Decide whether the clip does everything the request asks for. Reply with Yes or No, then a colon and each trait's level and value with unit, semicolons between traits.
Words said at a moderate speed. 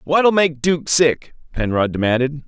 Yes: average, 145 wpm